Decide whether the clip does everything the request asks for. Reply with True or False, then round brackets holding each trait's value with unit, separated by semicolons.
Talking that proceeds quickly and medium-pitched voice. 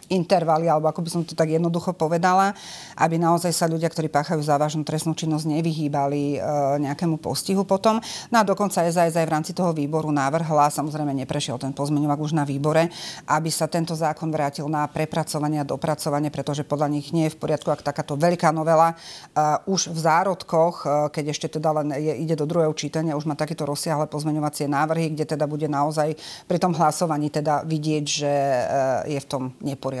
True (180 wpm; 155 Hz)